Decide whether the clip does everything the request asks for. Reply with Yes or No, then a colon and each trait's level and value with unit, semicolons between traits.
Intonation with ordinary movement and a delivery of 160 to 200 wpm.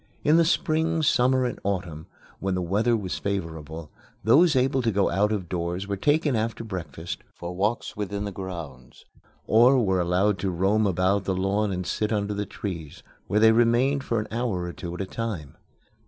Yes: average, 4.2 semitones; average, 190 wpm